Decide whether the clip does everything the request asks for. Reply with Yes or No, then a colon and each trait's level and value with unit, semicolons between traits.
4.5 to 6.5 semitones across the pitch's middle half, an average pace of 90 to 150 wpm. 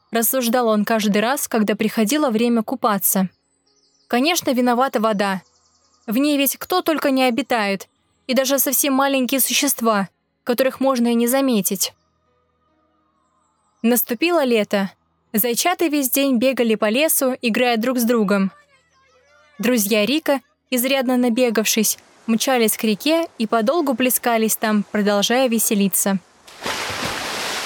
No: average, 3.8 semitones; average, 115 wpm